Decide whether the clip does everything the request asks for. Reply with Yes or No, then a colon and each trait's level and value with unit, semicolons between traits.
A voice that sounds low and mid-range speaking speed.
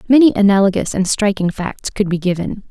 No: high, 200 Hz; average, 175 wpm